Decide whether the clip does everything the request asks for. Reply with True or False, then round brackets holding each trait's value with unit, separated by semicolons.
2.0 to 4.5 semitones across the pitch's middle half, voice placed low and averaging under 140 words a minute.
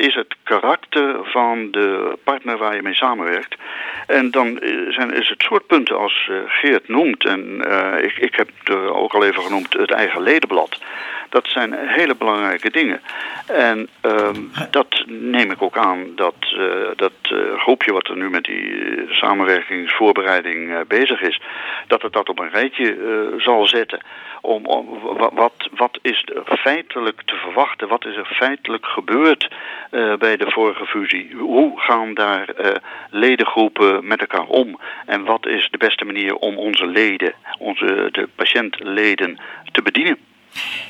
False (4.1 semitones; 115 Hz; 160 wpm)